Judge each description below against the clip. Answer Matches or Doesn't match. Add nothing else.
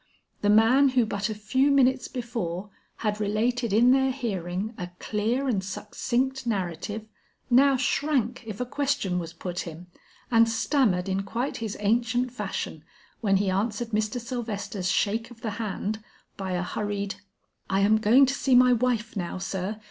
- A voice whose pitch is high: Matches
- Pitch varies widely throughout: Doesn't match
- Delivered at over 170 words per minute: Doesn't match